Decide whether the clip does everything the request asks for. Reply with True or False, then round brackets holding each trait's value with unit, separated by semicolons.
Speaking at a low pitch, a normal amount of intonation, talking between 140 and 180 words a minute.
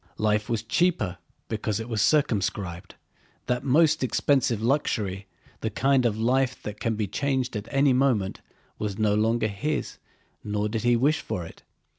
True (115 Hz; 4.0 semitones; 160 wpm)